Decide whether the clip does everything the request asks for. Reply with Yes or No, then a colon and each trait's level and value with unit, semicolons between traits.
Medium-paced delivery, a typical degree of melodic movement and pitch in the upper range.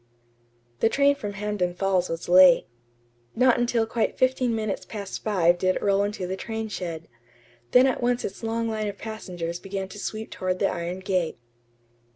Yes: average, 180 wpm; average, 3.5 semitones; high, 200 Hz